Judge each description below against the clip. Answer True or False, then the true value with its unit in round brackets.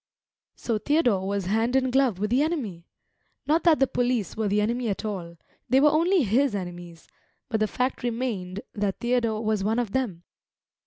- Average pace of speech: True (180 wpm)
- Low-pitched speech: False (225 Hz)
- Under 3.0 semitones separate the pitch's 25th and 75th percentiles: False (4.5 semitones)